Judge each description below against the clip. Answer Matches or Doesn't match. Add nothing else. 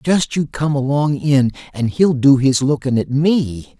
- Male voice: Matches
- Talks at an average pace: Matches